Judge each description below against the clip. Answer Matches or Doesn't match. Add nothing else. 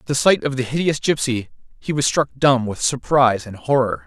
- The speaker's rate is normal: Doesn't match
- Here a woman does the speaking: Doesn't match